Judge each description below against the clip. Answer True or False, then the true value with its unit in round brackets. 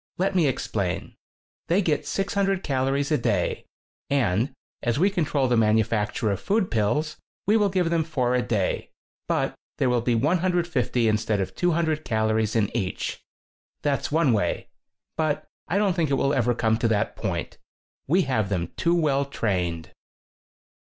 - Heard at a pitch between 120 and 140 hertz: True (135 Hz)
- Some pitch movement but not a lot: False (7.0 semitones)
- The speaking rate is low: False (160 wpm)